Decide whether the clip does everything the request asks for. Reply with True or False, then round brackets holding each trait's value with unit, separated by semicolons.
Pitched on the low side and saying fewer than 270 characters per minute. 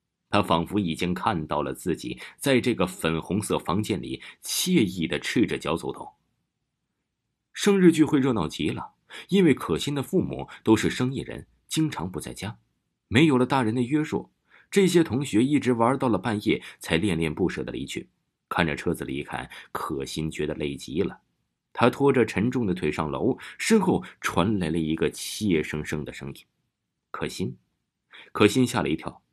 True (95 Hz; 250 characters per minute)